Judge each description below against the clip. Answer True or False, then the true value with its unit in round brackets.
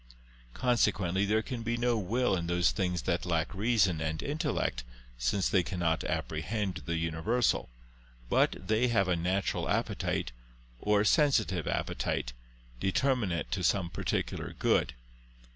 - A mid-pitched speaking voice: False (95 Hz)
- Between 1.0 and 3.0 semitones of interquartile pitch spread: False (5.0 semitones)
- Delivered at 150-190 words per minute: False (135 wpm)